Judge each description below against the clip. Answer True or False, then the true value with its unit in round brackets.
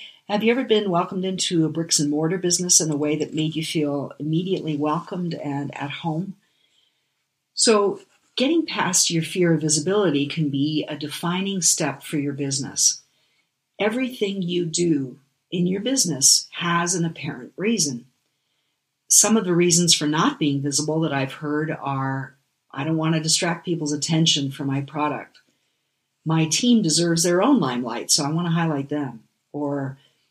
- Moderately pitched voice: True (155 Hz)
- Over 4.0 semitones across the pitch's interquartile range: False (3.2 semitones)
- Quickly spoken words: False (165 wpm)